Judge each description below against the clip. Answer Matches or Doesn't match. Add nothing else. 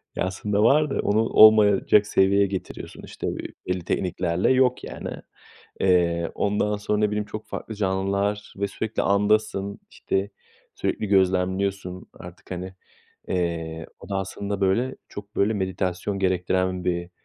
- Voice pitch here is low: Matches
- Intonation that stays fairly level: Matches